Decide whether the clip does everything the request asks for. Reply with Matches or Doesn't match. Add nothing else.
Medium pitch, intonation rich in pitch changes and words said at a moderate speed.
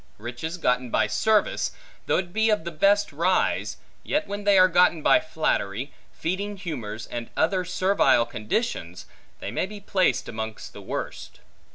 Matches